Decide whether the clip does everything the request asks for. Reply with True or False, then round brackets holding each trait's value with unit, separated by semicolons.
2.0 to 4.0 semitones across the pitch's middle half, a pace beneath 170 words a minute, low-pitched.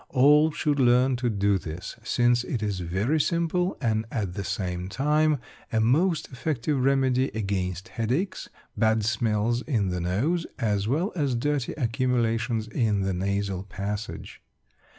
False (5.3 semitones; 145 wpm; 115 Hz)